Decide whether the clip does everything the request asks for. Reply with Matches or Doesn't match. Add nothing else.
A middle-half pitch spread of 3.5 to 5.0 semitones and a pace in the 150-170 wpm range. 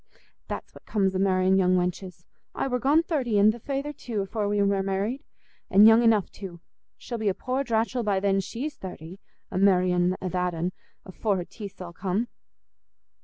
Doesn't match